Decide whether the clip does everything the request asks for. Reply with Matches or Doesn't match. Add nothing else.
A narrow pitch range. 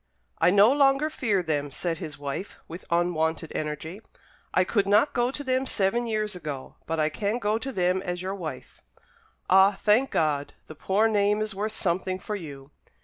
Doesn't match